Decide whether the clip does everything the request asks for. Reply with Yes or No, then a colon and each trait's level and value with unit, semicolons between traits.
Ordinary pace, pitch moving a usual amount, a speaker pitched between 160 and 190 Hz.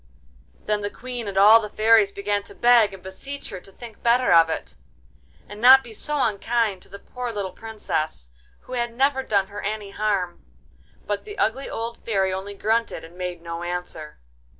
No: average, 190 wpm; average, 3.6 semitones; high, 210 Hz